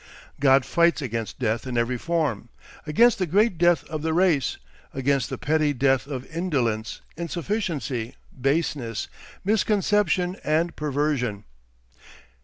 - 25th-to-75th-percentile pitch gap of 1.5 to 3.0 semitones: No, average, 5.2 semitones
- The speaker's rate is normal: No, slow, 120 wpm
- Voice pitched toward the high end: No, medium, 150 Hz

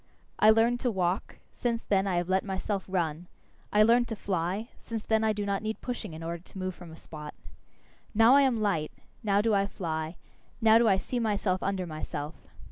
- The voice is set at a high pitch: Yes, high, 195 Hz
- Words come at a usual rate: No, fast, 210 wpm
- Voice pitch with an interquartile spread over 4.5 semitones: No, average, 4.0 semitones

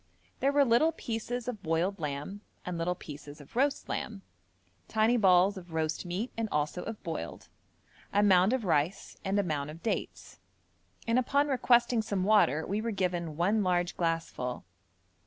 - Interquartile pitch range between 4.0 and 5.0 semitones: No, wide, 5.6 semitones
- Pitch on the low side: No, high, 195 Hz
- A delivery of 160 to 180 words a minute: Yes, average, 165 wpm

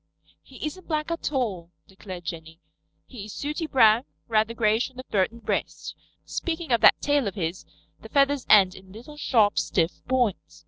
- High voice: Yes, high, 230 Hz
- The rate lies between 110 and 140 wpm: No, average, 180 wpm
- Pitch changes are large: Yes, wide, 6.7 semitones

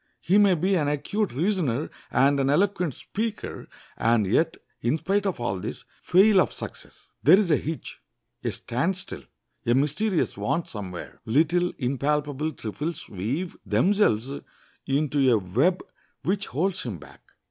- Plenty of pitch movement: Yes, wide, 6.6 semitones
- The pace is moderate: Yes, average, 145 wpm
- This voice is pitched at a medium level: Yes, medium, 150 Hz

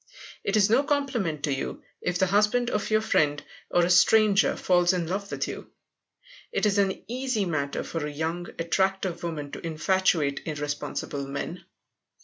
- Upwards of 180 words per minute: No, average, 165 wpm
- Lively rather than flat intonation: No, average, 4.8 semitones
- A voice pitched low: No, medium, 180 Hz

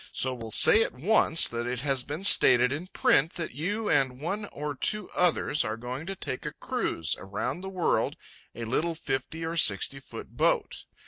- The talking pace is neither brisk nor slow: Yes, average, 190 wpm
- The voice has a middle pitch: Yes, medium, 145 Hz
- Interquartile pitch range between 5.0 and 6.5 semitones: Yes, wide, 5.4 semitones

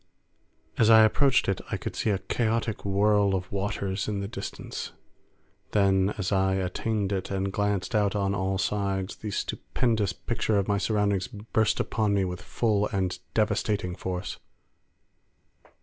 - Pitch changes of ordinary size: No, narrow, 1.9 semitones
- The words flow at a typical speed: Yes, average, 150 wpm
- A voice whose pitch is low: Yes, low, 100 Hz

